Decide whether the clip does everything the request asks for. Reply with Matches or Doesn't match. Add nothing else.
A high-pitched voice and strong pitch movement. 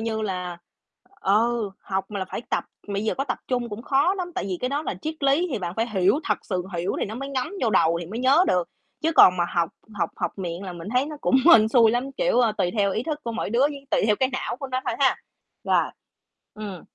Matches